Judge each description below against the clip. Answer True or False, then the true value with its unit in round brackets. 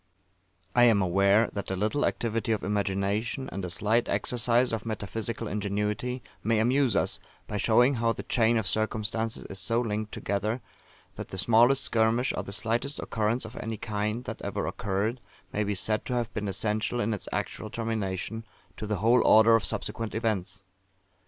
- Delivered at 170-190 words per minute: True (175 wpm)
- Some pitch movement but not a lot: False (2.1 semitones)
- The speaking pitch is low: True (110 Hz)